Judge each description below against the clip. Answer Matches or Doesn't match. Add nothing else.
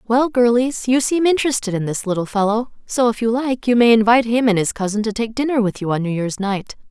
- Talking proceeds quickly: Matches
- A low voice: Doesn't match